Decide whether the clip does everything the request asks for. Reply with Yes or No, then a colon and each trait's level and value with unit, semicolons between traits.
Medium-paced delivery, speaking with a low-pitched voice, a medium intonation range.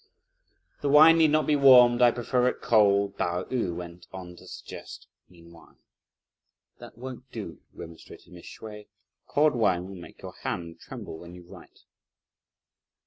No: average, 150 wpm; low, 105 Hz; wide, 6.3 semitones